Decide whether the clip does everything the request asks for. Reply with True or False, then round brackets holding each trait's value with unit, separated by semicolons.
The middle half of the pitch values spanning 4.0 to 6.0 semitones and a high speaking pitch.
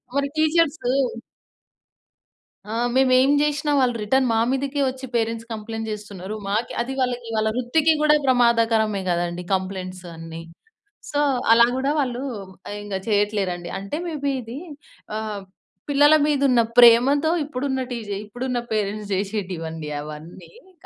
True (4.8 semitones; 230 Hz)